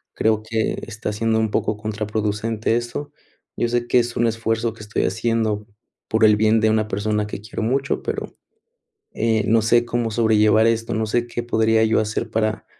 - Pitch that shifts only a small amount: Yes, narrow, 1.2 semitones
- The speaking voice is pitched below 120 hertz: Yes, low, 110 Hz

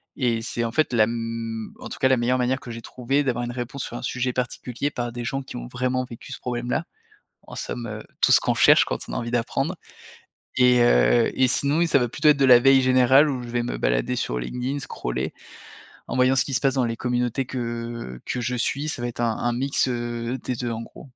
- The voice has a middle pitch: No, low, 125 Hz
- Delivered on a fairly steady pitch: Yes, narrow, 1.9 semitones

